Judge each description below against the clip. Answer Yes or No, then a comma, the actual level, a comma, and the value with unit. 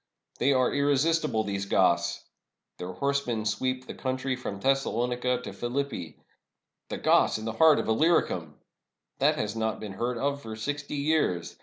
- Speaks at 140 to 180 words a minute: Yes, average, 160 wpm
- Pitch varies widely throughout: No, average, 4.3 semitones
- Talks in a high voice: No, low, 125 Hz